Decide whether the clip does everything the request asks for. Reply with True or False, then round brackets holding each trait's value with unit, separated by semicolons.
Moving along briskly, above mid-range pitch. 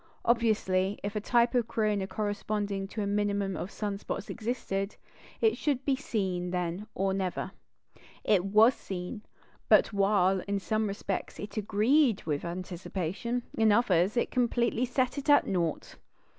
False (150 wpm; 205 Hz)